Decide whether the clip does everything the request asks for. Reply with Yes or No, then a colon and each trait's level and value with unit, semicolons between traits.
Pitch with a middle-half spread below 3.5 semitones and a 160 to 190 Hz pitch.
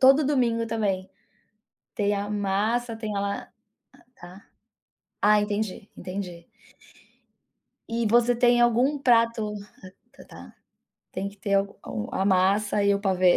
No: average, 2.7 semitones; high, 210 Hz